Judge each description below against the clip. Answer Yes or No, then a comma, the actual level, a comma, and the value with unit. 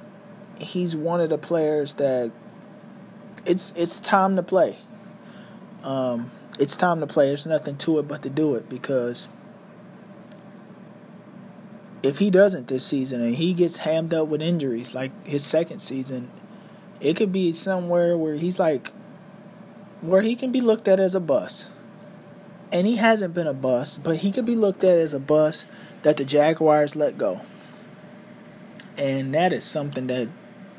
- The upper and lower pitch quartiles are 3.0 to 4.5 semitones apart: No, average, 4.9 semitones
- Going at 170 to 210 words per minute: No, average, 160 wpm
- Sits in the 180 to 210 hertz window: Yes, high, 190 Hz